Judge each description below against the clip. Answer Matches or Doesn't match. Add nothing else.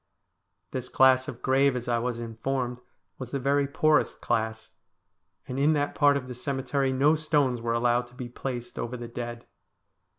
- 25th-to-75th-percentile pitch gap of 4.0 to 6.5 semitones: Doesn't match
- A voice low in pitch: Matches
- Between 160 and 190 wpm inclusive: Matches